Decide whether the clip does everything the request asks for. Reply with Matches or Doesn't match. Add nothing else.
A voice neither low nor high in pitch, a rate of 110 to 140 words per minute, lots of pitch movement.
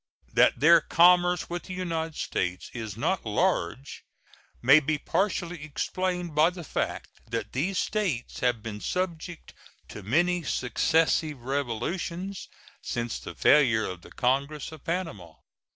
Matches